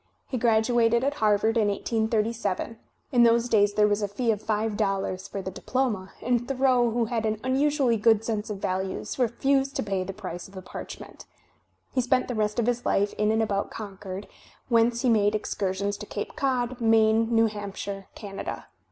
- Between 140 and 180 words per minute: No, average, 195 wpm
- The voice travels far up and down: No, average, 2.8 semitones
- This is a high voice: Yes, high, 220 Hz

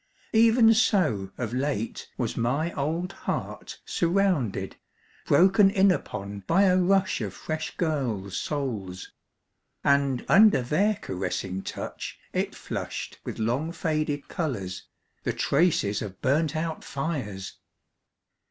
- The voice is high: No, medium, 150 Hz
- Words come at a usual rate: No, slow, 115 wpm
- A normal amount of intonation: No, wide, 8.5 semitones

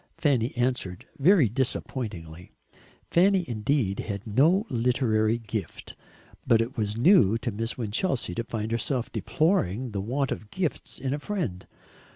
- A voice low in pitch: Yes, low, 120 Hz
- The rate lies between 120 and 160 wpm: Yes, average, 140 wpm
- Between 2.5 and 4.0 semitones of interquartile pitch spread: No, average, 4.7 semitones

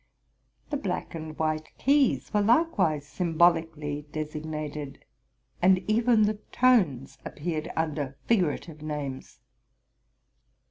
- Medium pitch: Yes, medium, 160 Hz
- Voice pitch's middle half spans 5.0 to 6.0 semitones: Yes, wide, 5.4 semitones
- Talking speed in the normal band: No, slow, 95 wpm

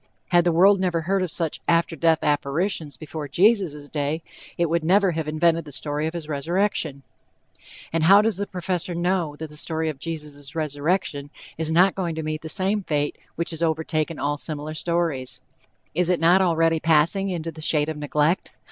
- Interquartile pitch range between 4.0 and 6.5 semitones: No, narrow, 2.6 semitones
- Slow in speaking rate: No, average, 190 wpm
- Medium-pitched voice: Yes, medium, 165 Hz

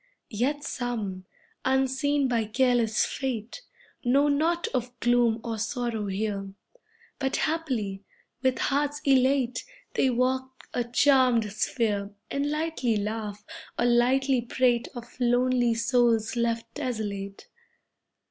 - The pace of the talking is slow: Yes, slow, 110 wpm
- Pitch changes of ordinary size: Yes, average, 3.0 semitones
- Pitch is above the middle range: Yes, high, 245 Hz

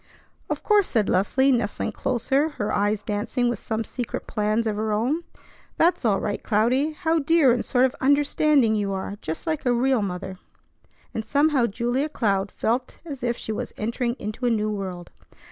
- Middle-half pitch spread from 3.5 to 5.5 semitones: Yes, average, 4.6 semitones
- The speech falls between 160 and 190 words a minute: Yes, average, 180 wpm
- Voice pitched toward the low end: No, high, 235 Hz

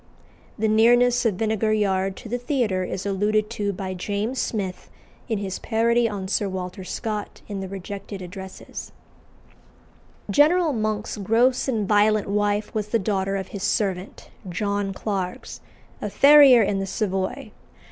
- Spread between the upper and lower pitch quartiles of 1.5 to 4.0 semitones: Yes, narrow, 2.6 semitones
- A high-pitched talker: Yes, high, 205 Hz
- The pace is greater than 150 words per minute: No, average, 145 wpm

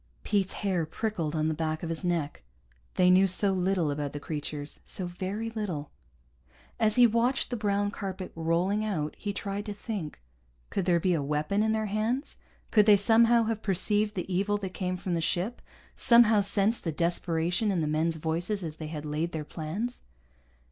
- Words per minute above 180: Yes, average, 190 wpm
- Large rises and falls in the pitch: No, average, 4.5 semitones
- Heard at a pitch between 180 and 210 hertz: Yes, medium, 185 Hz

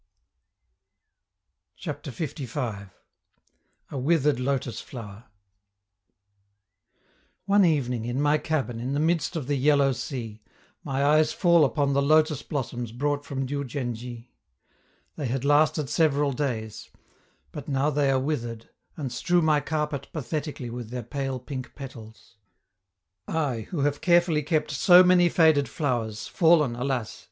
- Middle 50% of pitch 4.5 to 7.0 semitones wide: No, average, 3.6 semitones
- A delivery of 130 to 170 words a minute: Yes, slow, 135 wpm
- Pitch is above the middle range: No, medium, 140 Hz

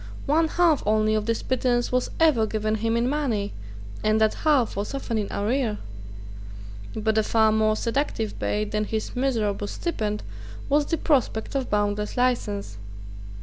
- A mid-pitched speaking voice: No, high, 220 Hz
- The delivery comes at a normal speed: Yes, average, 155 wpm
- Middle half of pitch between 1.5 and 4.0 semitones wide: Yes, average, 3.6 semitones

